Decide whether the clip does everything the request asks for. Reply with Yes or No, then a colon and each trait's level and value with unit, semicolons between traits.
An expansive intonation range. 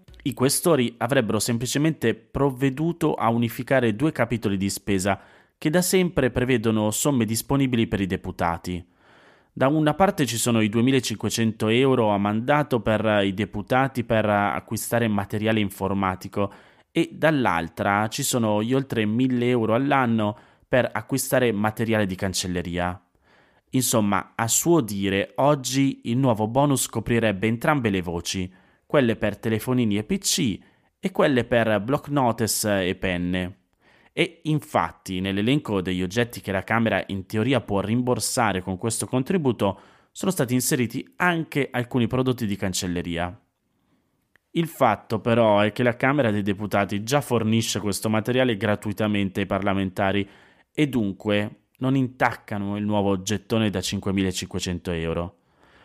No: average, 4.4 semitones